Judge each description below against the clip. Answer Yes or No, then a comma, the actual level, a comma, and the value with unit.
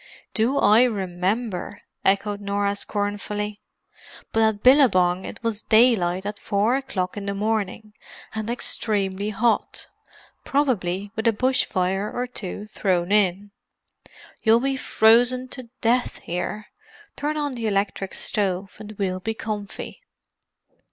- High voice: Yes, high, 210 Hz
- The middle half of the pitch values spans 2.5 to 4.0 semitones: Yes, average, 2.9 semitones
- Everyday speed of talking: No, slow, 125 wpm